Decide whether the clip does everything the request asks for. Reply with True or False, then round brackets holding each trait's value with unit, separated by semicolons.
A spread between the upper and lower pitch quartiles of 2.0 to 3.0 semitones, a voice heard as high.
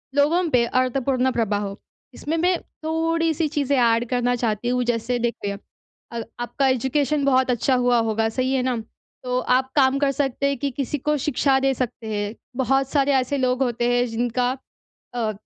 True (2.5 semitones; 255 Hz)